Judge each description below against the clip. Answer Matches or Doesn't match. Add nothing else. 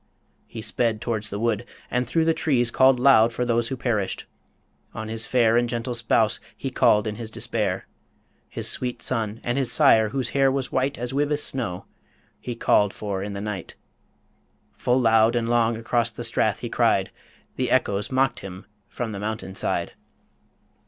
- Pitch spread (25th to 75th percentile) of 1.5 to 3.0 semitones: Matches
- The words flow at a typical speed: Matches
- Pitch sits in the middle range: Doesn't match